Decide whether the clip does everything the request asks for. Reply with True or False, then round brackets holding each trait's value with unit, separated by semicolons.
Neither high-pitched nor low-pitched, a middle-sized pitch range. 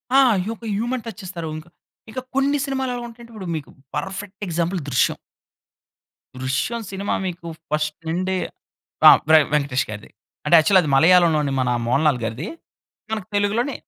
False (180 Hz; 6.5 semitones)